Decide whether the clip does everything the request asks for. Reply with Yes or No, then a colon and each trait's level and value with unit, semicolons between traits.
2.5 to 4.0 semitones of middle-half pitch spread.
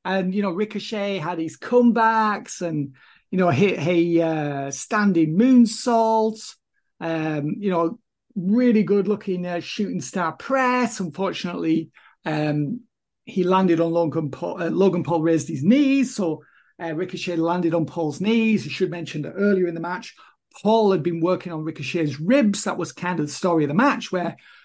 No: average, 4.4 semitones